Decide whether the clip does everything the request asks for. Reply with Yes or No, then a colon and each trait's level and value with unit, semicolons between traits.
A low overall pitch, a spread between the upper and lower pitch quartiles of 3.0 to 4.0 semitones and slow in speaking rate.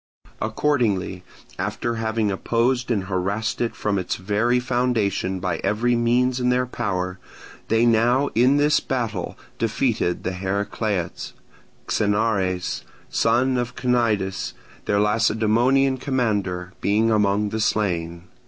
Yes: low, 110 Hz; average, 3.7 semitones; slow, 115 wpm